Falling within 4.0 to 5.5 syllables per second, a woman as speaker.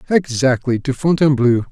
No: 5.4 syllables/s; male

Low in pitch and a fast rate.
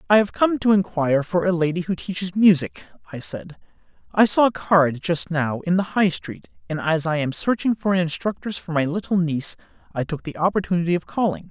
No: medium, 175 Hz; fast, 215 wpm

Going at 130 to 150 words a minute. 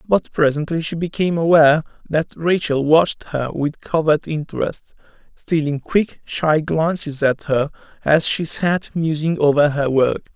Yes: average, 145 wpm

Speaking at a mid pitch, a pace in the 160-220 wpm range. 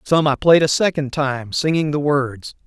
Yes: medium, 145 Hz; fast, 205 wpm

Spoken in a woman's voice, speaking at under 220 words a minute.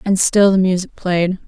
Yes: female; fast, 205 wpm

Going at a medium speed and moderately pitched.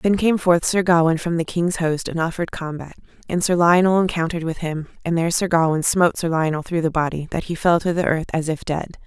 No: fast, 245 wpm; medium, 170 Hz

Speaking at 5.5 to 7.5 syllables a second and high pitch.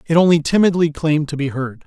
No: 6.3 syllables/s; medium, 155 Hz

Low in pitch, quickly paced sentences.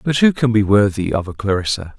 Yes: low, 105 Hz; fast, 240 wpm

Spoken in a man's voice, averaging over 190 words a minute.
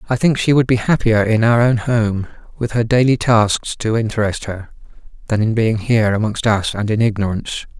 Yes: male; average, 200 wpm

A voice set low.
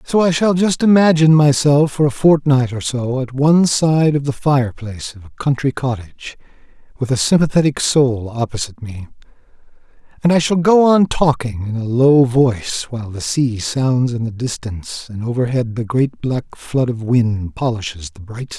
Yes: low, 130 Hz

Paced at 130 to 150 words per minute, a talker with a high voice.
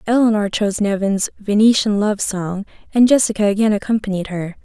Yes: average, 140 wpm; high, 205 Hz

